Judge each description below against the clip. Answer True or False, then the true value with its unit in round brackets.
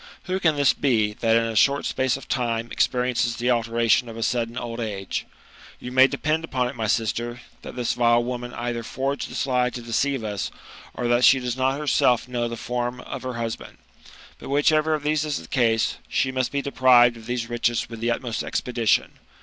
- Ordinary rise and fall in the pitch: False (2.0 semitones)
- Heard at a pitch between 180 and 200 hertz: False (120 Hz)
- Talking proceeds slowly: False (205 wpm)